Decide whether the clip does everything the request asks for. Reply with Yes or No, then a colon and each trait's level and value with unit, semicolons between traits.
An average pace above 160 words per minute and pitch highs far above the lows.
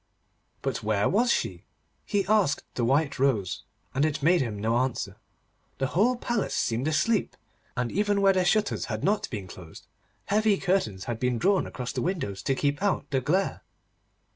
Yes: average, 175 wpm; wide, 8.6 semitones